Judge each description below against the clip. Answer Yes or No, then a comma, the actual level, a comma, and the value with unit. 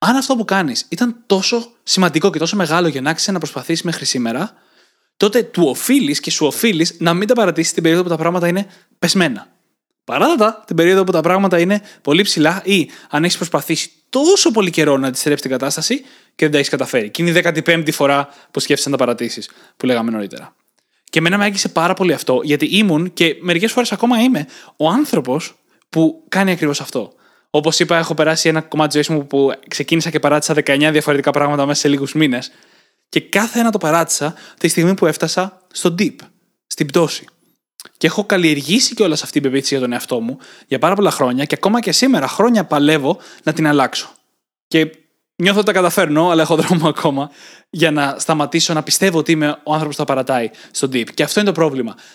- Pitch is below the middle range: No, medium, 165 Hz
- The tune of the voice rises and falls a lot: No, average, 4.6 semitones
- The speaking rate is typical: No, fast, 205 wpm